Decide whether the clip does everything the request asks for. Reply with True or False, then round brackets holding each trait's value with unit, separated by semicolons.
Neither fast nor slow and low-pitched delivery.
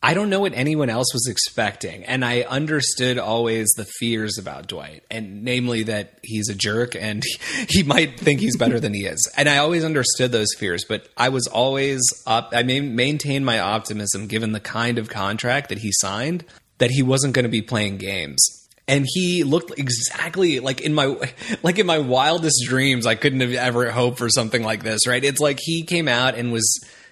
False (210 wpm; 125 Hz)